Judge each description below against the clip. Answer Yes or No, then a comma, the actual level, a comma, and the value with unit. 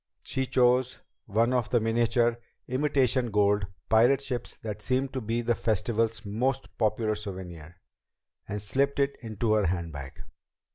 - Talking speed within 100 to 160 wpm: Yes, average, 140 wpm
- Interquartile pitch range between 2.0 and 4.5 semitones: Yes, average, 3.4 semitones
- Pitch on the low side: Yes, low, 115 Hz